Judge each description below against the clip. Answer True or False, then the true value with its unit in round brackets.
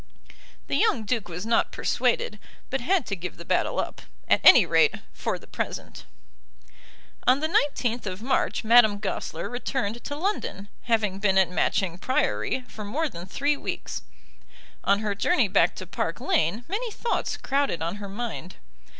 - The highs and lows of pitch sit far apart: True (6.0 semitones)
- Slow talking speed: False (165 wpm)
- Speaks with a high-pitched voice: True (220 Hz)